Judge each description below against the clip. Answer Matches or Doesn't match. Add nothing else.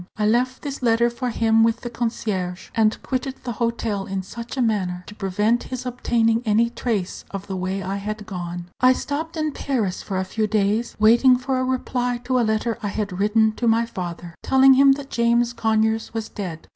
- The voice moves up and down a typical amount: Matches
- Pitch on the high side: Matches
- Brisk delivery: Matches